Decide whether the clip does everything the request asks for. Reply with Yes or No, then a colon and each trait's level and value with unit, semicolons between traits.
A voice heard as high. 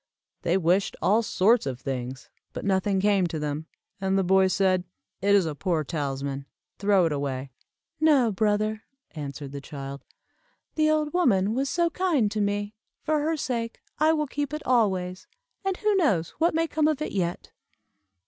Yes: high, 200 Hz